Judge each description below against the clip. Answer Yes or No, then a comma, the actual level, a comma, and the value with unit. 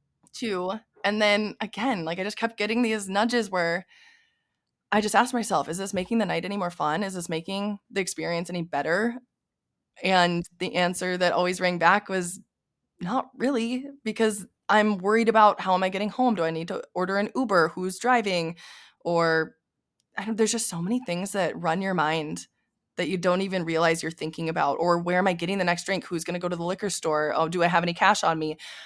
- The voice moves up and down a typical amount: Yes, average, 3.7 semitones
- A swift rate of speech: Yes, fast, 215 wpm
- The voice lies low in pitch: No, medium, 185 Hz